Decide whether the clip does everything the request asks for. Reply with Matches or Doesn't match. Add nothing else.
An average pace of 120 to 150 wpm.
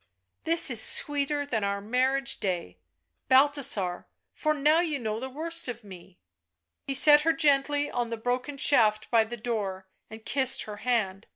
Doesn't match